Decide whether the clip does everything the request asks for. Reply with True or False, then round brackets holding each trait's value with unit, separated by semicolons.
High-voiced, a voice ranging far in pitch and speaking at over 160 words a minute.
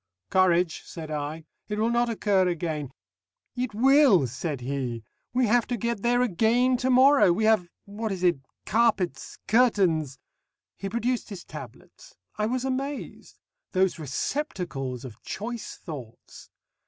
False (200 Hz; 7.1 semitones; 140 wpm)